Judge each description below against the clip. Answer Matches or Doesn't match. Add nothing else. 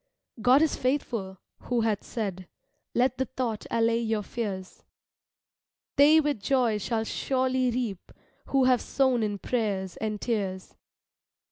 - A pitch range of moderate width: Matches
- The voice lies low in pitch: Doesn't match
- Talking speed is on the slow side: Matches